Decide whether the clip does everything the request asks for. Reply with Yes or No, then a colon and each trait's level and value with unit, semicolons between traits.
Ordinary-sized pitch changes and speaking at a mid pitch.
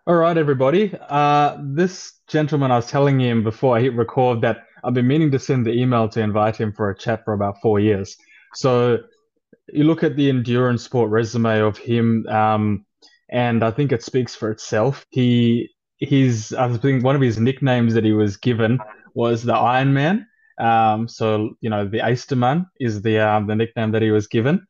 No: average, 3.8 semitones; low, 120 Hz